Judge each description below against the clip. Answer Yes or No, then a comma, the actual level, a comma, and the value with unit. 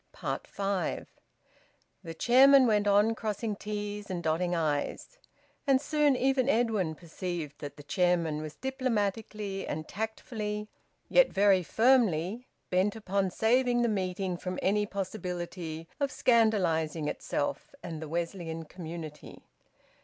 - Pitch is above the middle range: Yes, high, 195 Hz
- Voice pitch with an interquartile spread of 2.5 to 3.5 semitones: No, average, 4.8 semitones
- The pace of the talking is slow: Yes, slow, 120 wpm